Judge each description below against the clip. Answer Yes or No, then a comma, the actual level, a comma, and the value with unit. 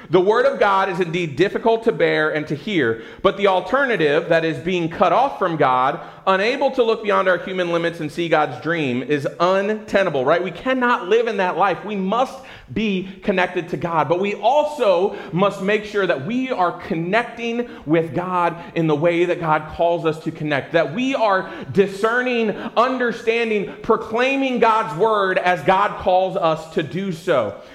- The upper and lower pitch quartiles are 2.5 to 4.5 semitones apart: No, average, 4.9 semitones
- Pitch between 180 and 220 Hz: Yes, high, 190 Hz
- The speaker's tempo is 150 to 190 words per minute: Yes, average, 180 wpm